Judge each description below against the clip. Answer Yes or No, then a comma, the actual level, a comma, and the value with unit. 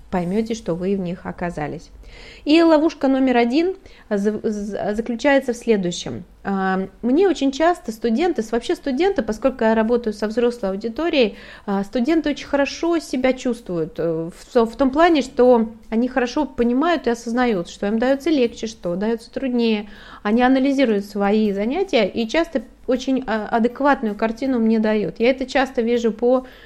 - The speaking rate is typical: Yes, average, 140 wpm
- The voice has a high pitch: Yes, high, 235 Hz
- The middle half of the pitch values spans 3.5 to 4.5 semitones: Yes, average, 4.0 semitones